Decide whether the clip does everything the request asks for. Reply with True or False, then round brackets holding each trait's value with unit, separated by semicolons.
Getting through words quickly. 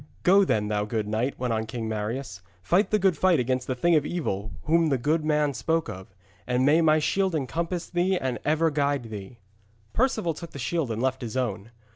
True (210 wpm)